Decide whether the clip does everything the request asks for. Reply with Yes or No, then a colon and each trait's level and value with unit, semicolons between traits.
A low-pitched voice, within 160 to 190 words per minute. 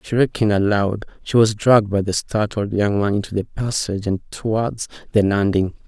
Yes: low, 105 Hz; average, 175 wpm